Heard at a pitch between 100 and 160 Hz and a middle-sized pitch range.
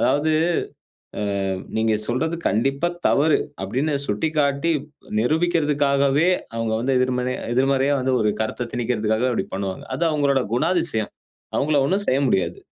Yes: low, 135 Hz; average, 4.5 semitones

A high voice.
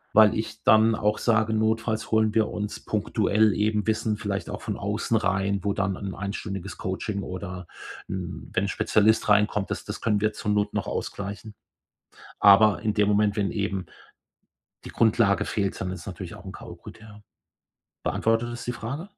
No: low, 105 Hz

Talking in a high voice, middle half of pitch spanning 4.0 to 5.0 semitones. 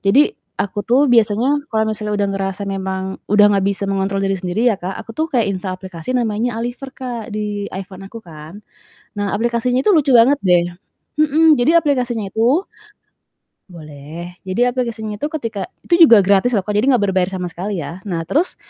Yes: high, 210 Hz; average, 4.4 semitones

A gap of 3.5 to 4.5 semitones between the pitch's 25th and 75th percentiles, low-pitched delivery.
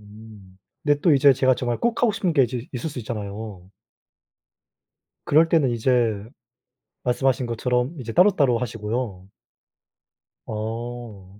Yes: average, 4.0 semitones; low, 120 Hz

